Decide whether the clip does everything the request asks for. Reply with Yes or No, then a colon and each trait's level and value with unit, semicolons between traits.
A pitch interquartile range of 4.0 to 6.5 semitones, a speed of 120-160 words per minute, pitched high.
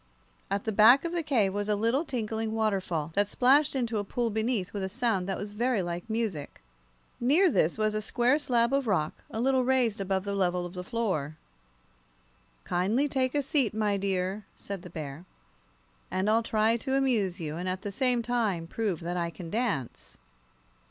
No: average, 4.5 semitones; average, 190 wpm; high, 215 Hz